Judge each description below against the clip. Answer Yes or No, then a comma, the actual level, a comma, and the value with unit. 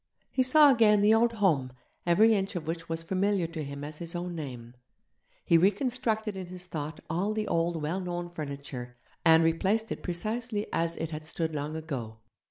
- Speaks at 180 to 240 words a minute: Yes, average, 185 wpm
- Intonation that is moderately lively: Yes, average, 4.9 semitones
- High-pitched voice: No, medium, 170 Hz